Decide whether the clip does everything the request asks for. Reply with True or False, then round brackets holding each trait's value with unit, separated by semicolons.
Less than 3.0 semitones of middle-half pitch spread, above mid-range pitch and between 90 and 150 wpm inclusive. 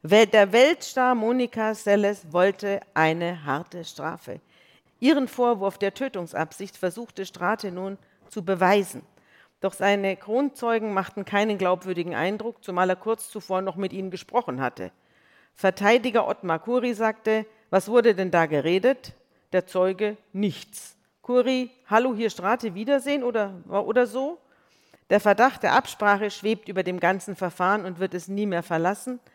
False (3.8 semitones; 205 Hz; 140 wpm)